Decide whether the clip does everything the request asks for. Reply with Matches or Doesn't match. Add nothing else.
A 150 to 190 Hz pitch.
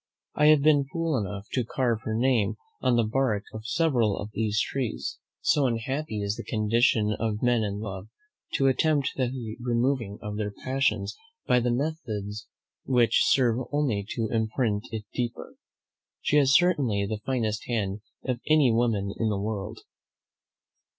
Doesn't match